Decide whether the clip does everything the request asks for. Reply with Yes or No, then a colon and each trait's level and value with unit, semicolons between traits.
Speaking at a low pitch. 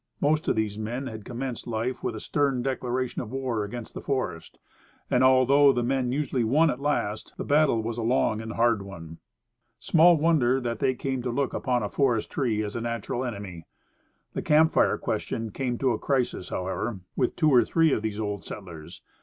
Yes: low, 120 Hz